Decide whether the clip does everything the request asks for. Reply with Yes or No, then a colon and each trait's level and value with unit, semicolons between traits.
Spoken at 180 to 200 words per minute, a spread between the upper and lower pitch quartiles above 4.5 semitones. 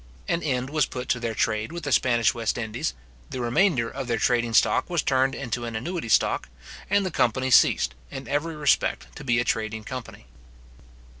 No: average, 195 wpm; average, 3.7 semitones